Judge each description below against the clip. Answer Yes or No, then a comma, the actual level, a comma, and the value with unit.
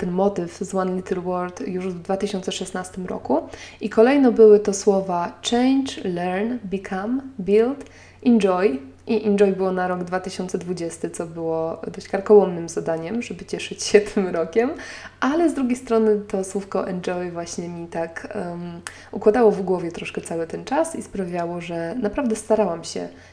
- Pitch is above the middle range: Yes, high, 195 Hz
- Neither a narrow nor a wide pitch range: Yes, average, 3.2 semitones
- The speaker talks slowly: No, average, 155 wpm